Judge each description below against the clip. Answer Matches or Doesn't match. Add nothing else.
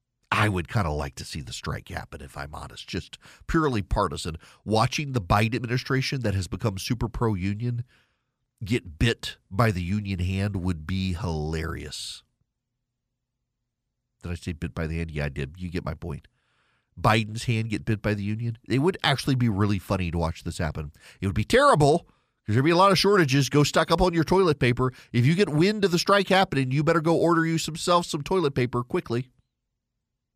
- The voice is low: Matches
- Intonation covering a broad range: Matches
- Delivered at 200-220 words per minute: Matches